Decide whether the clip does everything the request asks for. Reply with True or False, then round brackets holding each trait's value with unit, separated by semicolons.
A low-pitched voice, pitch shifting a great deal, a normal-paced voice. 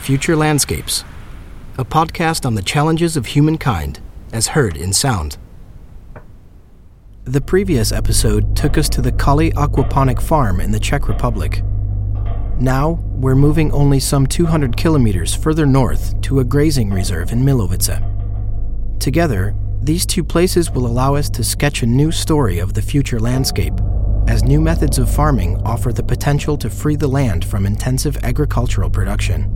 True (115 Hz; 6.2 semitones; 150 wpm)